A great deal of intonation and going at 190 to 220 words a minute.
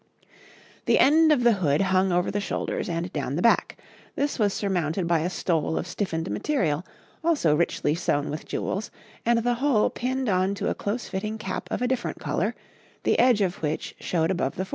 Yes: wide, 6.0 semitones; average, 200 wpm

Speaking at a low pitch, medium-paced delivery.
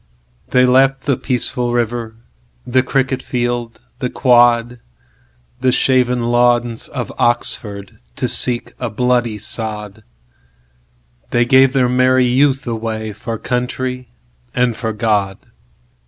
No: low, 120 Hz; slow, 95 wpm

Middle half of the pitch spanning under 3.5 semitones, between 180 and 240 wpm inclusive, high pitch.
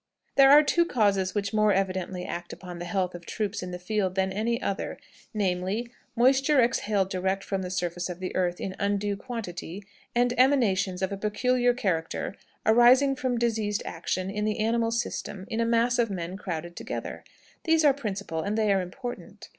No: average, 4.2 semitones; average, 185 wpm; high, 205 Hz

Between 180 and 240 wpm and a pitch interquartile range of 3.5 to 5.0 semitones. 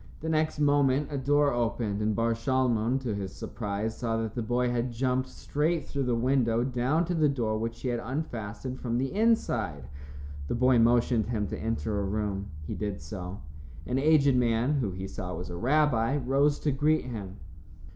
Yes: average, 190 wpm; average, 3.9 semitones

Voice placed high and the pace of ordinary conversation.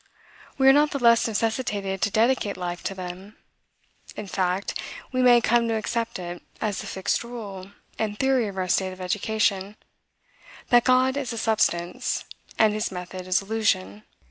Yes: high, 210 Hz; average, 170 wpm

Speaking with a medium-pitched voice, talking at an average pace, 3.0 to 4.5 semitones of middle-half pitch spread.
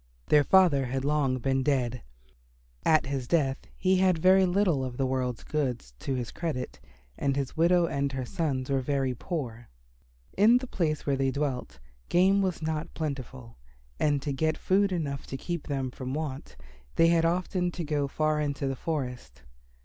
Yes: medium, 145 Hz; average, 170 wpm; average, 4.1 semitones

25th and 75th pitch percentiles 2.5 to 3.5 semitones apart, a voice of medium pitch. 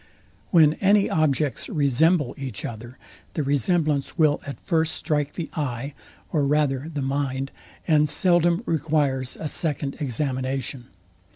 Yes: average, 2.9 semitones; medium, 145 Hz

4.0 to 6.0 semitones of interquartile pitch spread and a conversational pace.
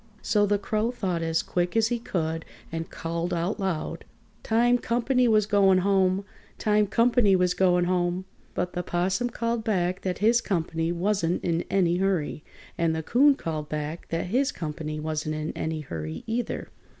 Yes: average, 4.5 semitones; average, 170 wpm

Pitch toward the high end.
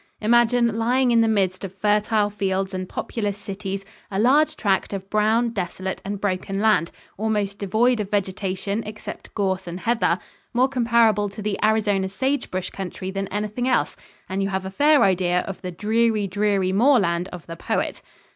Yes: high, 205 Hz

